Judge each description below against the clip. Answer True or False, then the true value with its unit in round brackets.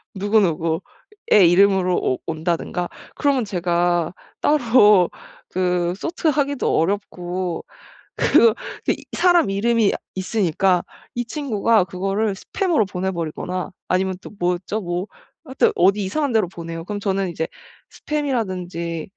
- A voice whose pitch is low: False (190 Hz)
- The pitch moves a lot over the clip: False (4.1 semitones)